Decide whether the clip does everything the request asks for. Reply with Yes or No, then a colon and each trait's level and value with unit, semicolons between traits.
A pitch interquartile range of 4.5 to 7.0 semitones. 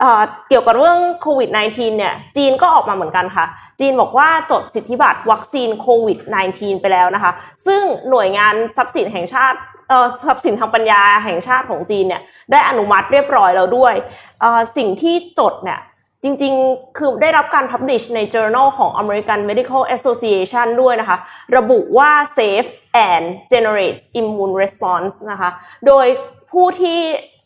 Yes: average, 4.9 semitones